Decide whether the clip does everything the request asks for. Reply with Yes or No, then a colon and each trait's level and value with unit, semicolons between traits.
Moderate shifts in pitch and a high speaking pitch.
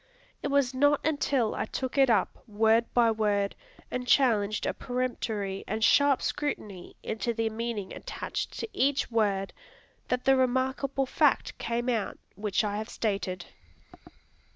Yes: average, 3.7 semitones; high, 230 Hz